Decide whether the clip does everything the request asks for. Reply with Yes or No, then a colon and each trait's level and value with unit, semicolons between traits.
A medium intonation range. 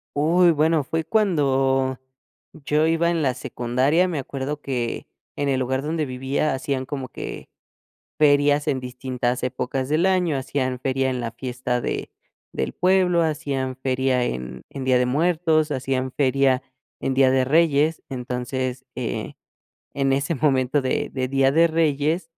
Yes: average, 3.0 semitones